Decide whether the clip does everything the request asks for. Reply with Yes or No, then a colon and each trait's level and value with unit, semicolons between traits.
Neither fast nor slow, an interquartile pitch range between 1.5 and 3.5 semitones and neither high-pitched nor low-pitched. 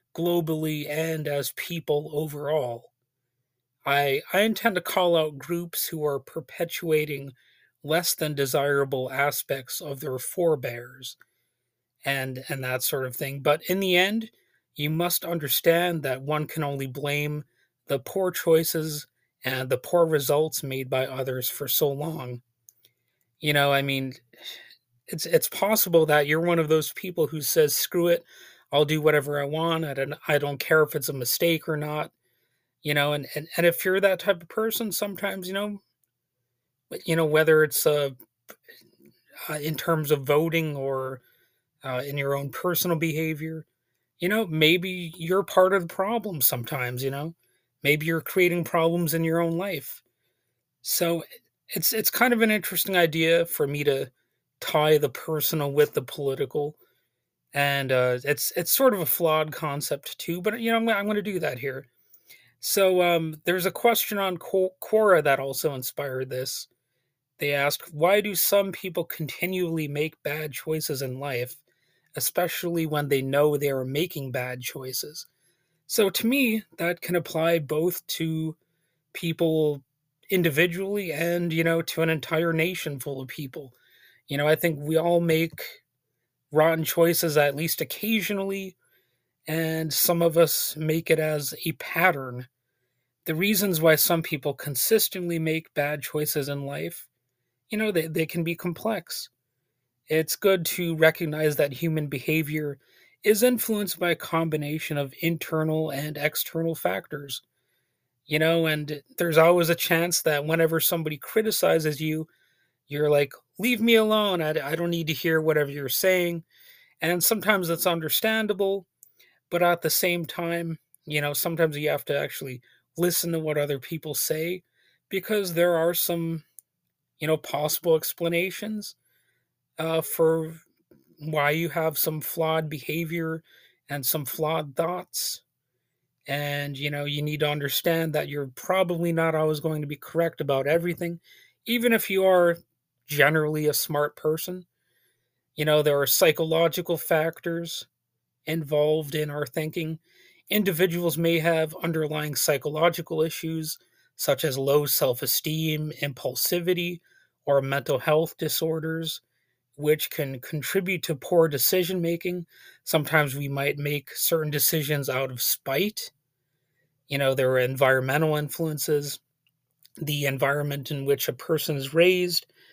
Yes: average, 150 wpm; average, 3.1 semitones; medium, 155 Hz